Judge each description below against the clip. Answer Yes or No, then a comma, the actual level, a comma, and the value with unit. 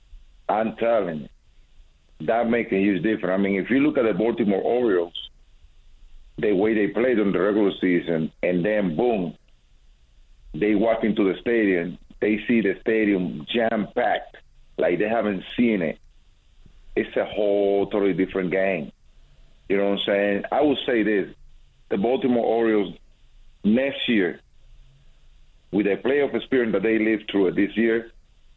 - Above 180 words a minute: No, average, 160 wpm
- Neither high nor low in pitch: No, very low, 95 Hz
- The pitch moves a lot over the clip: Yes, wide, 6.2 semitones